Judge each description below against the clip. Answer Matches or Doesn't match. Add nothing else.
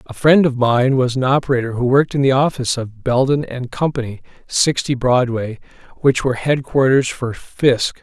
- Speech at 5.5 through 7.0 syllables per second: Doesn't match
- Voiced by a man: Matches